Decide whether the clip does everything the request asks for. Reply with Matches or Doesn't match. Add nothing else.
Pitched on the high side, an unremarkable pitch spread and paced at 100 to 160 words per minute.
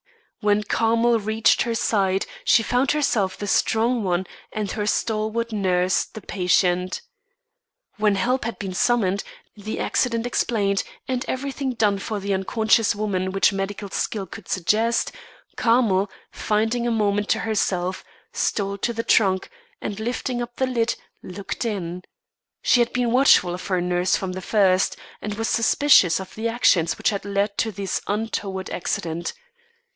Matches